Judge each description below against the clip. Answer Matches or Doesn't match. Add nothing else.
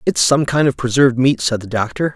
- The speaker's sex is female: Doesn't match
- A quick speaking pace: Matches